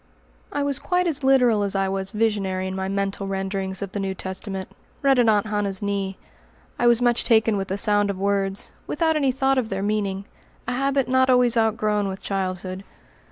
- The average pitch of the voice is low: No, high, 205 Hz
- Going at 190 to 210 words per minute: Yes, average, 200 wpm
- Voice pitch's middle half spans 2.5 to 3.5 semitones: No, average, 4.2 semitones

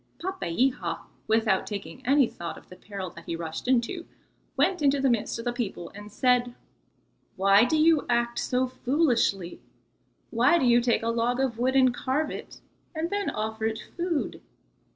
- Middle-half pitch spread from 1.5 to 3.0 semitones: No, average, 4.1 semitones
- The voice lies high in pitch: Yes, high, 240 Hz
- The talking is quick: No, average, 175 wpm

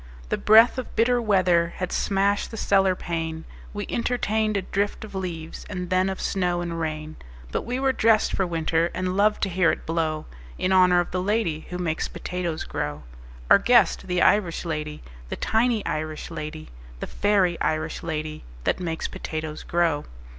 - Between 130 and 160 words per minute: No, average, 175 wpm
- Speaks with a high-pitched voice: No, medium, 180 Hz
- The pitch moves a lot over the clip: No, average, 3.9 semitones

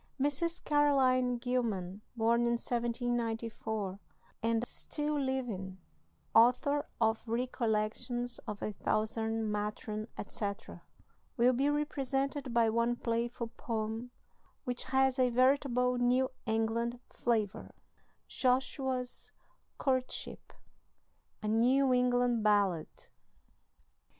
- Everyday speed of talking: No, slow, 90 wpm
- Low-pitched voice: No, high, 240 Hz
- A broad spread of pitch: No, narrow, 2.5 semitones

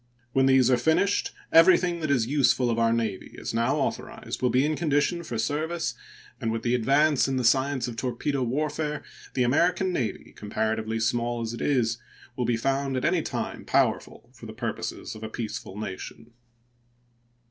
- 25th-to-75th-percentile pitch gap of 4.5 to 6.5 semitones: No, average, 4.1 semitones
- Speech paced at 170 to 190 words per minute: Yes, average, 180 wpm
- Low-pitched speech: Yes, low, 125 Hz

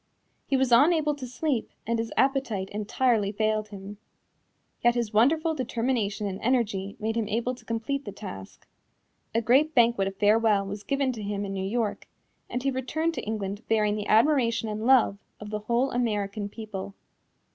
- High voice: Yes, high, 225 Hz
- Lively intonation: No, average, 3.7 semitones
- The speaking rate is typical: Yes, average, 175 wpm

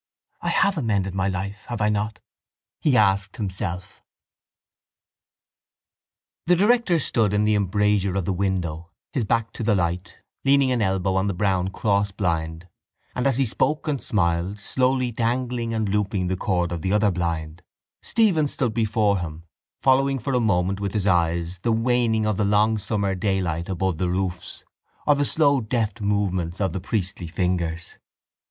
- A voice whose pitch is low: Yes, low, 100 Hz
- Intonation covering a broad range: No, average, 4.1 semitones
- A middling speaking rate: Yes, average, 165 wpm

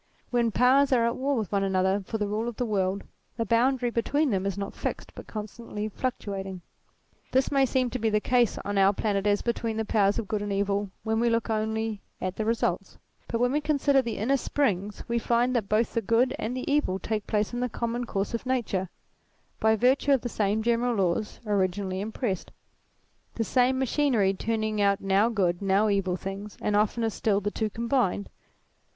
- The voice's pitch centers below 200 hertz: No, high, 220 Hz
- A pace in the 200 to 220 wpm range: Yes, fast, 205 wpm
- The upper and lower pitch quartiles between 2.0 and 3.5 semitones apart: Yes, average, 3.2 semitones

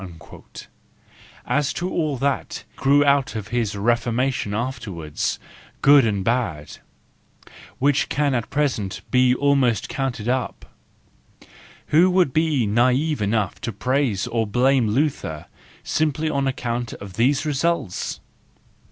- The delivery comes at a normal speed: No, slow, 115 wpm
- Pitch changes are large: No, average, 4.2 semitones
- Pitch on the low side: Yes, low, 130 Hz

